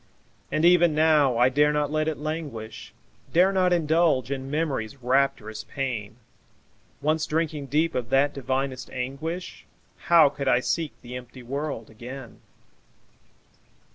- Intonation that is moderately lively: Yes, average, 3.8 semitones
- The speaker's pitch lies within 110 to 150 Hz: Yes, medium, 140 Hz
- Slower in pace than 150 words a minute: Yes, slow, 135 wpm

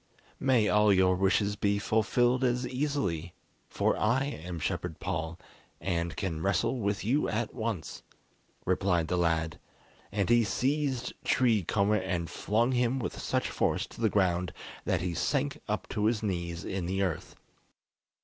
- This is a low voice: Yes, low, 100 Hz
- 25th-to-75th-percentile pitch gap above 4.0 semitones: Yes, average, 5.0 semitones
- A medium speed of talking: Yes, average, 155 wpm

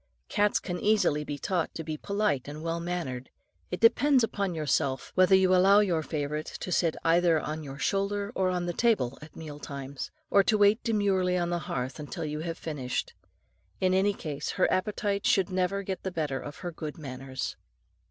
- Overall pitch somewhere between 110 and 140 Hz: No, medium, 175 Hz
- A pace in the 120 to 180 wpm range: No, average, 190 wpm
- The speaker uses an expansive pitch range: No, average, 4.7 semitones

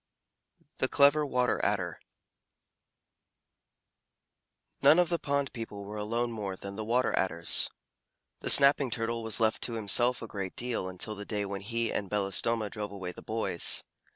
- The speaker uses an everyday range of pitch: Yes, average, 3.4 semitones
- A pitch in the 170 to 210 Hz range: No, low, 110 Hz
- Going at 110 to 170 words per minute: Yes, average, 155 wpm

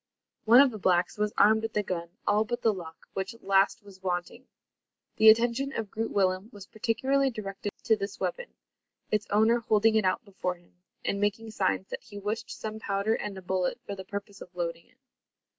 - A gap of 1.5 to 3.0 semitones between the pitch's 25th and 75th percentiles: Yes, average, 2.7 semitones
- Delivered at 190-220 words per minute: Yes, average, 200 wpm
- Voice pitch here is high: Yes, high, 205 Hz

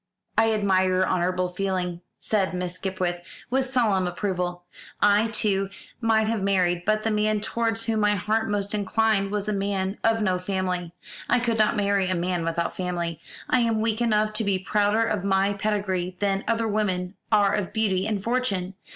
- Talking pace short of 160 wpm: No, average, 180 wpm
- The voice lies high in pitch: Yes, high, 200 Hz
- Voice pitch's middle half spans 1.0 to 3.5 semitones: Yes, average, 2.8 semitones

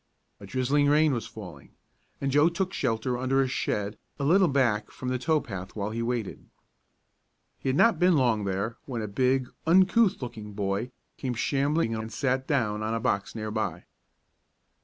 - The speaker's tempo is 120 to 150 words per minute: No, average, 180 wpm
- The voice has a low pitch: Yes, low, 125 Hz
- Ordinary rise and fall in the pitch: Yes, average, 4.8 semitones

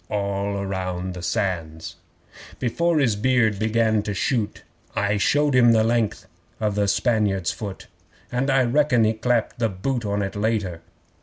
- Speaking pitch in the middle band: No, low, 110 Hz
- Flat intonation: No, average, 3.3 semitones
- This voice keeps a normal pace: Yes, average, 155 wpm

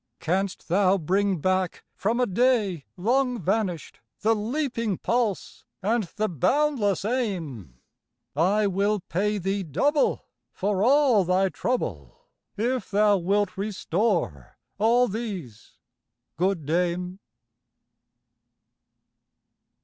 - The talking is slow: Yes, slow, 100 wpm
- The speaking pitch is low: No, high, 200 Hz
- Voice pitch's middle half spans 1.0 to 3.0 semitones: No, average, 4.0 semitones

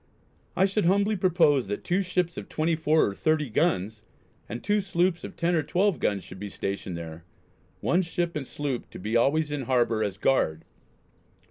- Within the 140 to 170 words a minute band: No, average, 180 wpm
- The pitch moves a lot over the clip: Yes, wide, 8.3 semitones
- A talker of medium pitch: Yes, medium, 150 Hz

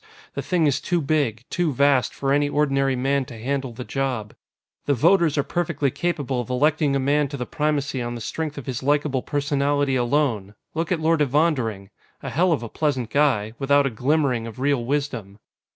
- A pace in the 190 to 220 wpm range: Yes, average, 195 wpm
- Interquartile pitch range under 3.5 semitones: Yes, average, 3.1 semitones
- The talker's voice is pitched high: No, medium, 140 Hz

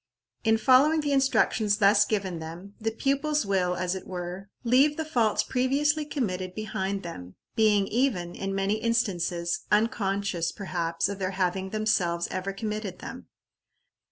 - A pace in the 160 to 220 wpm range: No, average, 145 wpm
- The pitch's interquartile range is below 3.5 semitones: No, average, 4.1 semitones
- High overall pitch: Yes, high, 200 Hz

